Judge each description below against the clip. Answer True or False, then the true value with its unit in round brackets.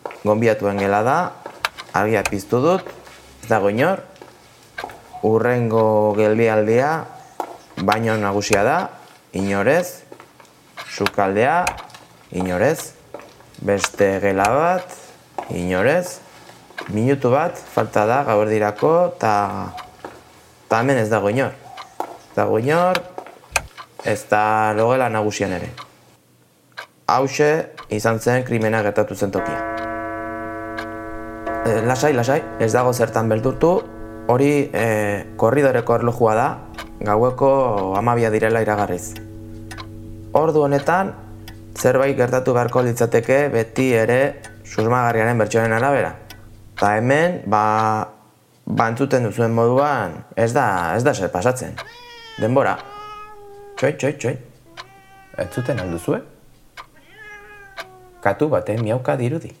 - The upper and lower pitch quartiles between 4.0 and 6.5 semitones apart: False (3.5 semitones)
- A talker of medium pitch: False (115 Hz)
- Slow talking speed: True (100 wpm)